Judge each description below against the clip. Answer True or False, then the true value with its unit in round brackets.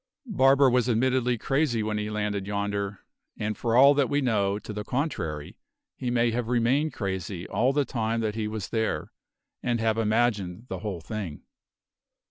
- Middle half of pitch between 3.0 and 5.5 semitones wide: True (3.3 semitones)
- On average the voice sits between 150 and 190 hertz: False (110 Hz)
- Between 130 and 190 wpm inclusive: True (170 wpm)